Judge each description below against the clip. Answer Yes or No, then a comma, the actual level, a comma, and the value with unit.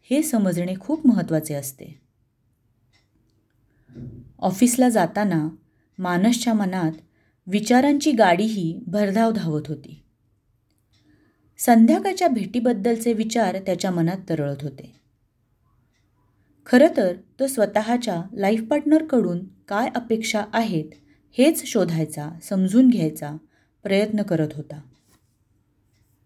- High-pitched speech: No, medium, 180 Hz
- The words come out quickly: No, average, 85 wpm